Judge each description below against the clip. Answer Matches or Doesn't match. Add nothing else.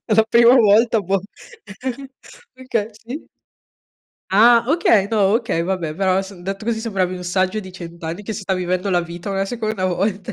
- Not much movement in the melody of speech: Doesn't match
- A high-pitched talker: Matches